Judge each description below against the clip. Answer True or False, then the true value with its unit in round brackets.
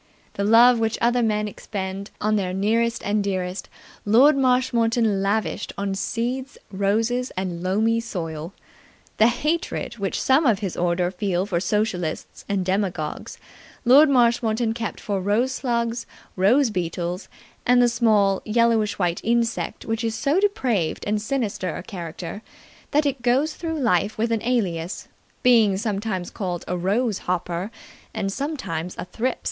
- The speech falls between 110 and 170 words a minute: True (145 wpm)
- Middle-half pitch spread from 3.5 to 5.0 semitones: True (4.0 semitones)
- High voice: True (215 Hz)